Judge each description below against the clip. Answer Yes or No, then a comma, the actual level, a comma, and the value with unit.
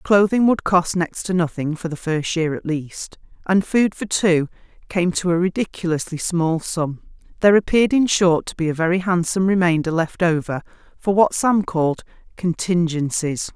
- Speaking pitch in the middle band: Yes, medium, 175 Hz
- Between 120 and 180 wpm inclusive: Yes, average, 170 wpm